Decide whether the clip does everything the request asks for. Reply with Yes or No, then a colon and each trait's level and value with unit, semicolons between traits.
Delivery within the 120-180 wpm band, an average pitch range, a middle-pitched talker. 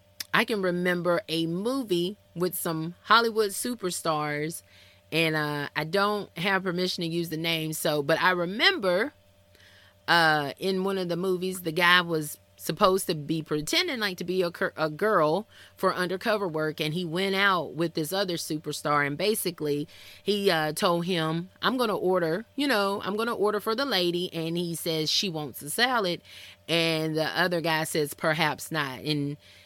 Yes: average, 170 wpm; average, 3.7 semitones; medium, 170 Hz